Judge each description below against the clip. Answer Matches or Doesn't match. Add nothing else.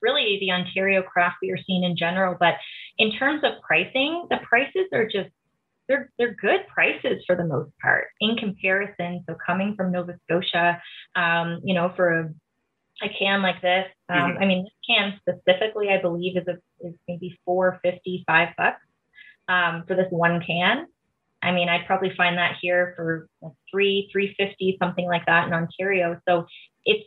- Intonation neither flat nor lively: Doesn't match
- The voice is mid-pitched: Matches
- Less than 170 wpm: Doesn't match